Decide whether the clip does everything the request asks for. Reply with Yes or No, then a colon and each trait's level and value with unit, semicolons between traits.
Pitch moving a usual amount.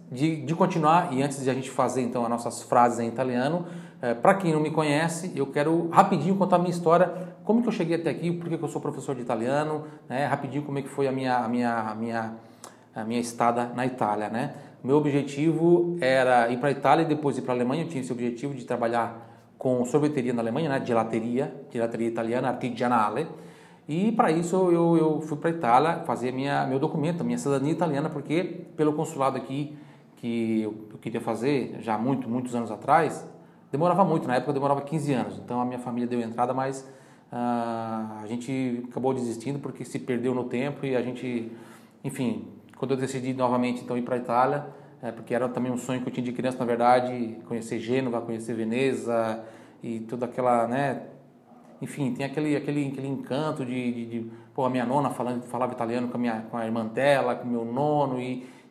Yes: average, 3.4 semitones